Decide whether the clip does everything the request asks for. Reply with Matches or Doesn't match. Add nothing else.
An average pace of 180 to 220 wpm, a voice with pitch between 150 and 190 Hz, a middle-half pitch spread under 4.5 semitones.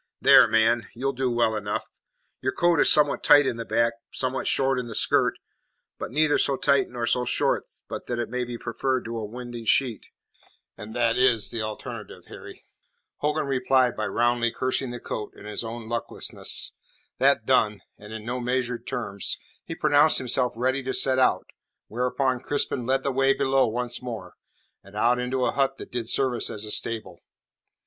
Doesn't match